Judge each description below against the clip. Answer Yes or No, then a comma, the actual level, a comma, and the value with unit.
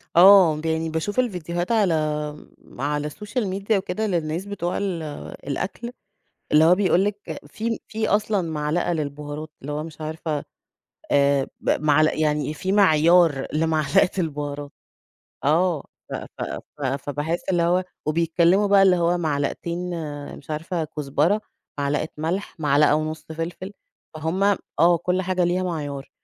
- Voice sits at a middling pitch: Yes, medium, 165 Hz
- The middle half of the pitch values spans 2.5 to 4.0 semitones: Yes, average, 3.6 semitones